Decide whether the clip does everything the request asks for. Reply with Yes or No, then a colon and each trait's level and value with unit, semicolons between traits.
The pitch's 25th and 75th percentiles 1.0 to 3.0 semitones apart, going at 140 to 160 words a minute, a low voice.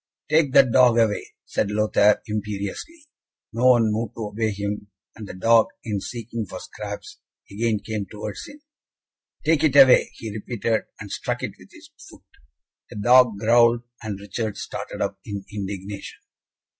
Yes: narrow, 2.6 semitones; average, 155 wpm; low, 110 Hz